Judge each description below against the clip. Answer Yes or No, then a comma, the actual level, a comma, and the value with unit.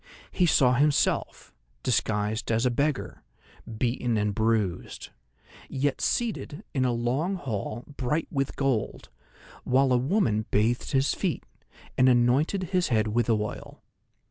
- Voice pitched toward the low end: Yes, low, 125 Hz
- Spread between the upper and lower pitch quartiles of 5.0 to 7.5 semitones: No, average, 4.0 semitones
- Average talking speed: No, slow, 130 wpm